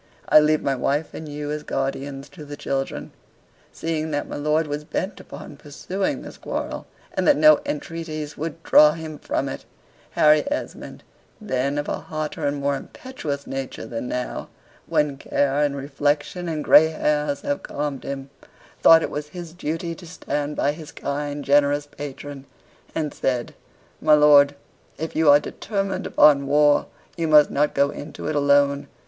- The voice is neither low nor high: Yes, medium, 150 Hz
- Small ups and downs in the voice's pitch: Yes, narrow, 1.6 semitones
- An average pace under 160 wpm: No, average, 165 wpm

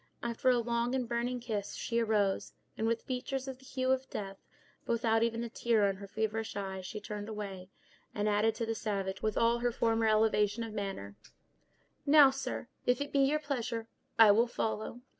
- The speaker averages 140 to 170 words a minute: No, average, 195 wpm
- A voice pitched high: Yes, high, 225 Hz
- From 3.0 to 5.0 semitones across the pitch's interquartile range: No, narrow, 2.6 semitones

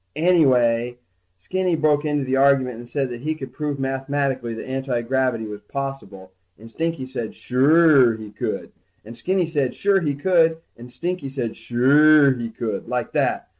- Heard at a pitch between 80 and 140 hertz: Yes, low, 135 Hz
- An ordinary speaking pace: Yes, average, 165 wpm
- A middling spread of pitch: Yes, average, 4.1 semitones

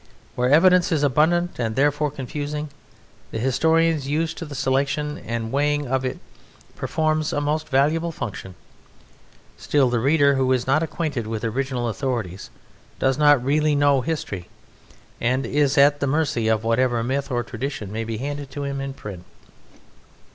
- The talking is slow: No, average, 160 wpm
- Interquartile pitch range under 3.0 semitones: No, average, 3.3 semitones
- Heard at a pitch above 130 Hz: Yes, medium, 140 Hz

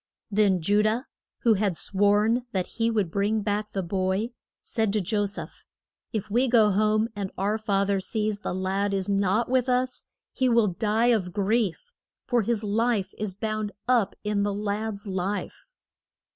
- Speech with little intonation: Yes, narrow, 2.1 semitones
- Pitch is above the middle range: Yes, high, 210 Hz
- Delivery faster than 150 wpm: Yes, average, 170 wpm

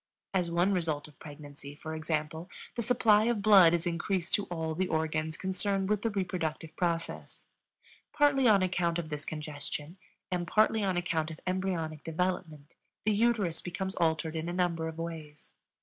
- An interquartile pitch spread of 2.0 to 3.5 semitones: Yes, average, 3.2 semitones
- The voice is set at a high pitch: No, medium, 170 Hz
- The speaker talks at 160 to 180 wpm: Yes, average, 165 wpm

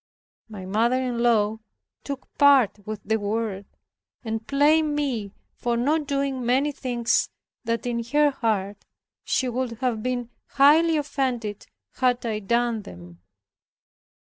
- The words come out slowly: Yes, slow, 130 wpm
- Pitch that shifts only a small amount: No, average, 3.9 semitones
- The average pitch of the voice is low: No, high, 240 Hz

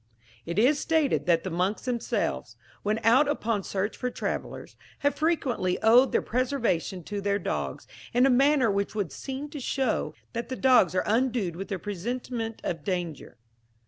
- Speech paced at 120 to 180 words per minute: Yes, average, 170 wpm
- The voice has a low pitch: No, high, 225 Hz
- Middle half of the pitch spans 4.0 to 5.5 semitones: Yes, average, 5.2 semitones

